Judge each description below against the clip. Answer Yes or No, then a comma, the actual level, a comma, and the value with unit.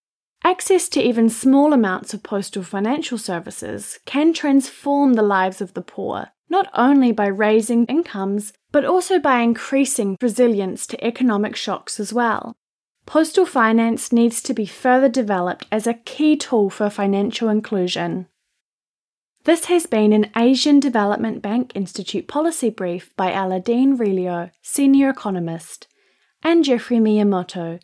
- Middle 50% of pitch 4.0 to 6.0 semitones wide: Yes, average, 5.2 semitones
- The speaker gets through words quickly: No, slow, 135 wpm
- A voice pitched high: Yes, high, 230 Hz